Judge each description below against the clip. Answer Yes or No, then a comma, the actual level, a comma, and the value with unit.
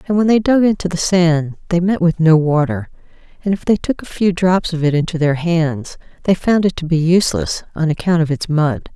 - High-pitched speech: No, medium, 170 Hz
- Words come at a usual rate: No, fast, 235 wpm